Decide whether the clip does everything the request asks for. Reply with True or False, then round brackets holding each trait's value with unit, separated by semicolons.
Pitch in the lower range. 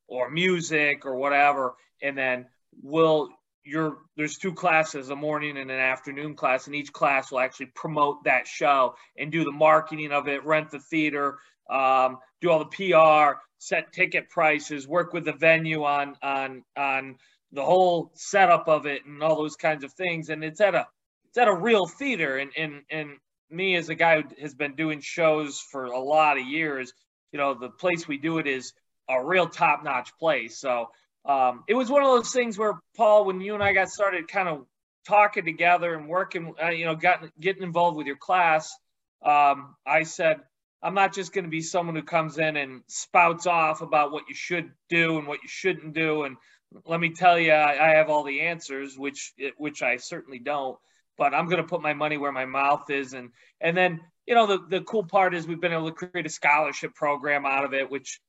False (155 Hz)